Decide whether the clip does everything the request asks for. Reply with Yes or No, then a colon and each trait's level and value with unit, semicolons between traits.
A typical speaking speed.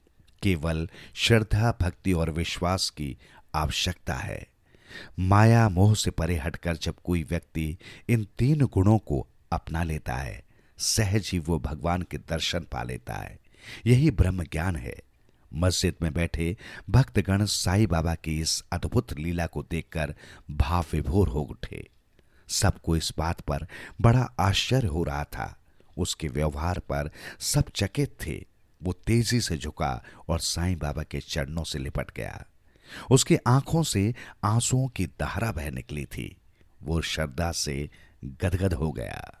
Yes: average, 140 wpm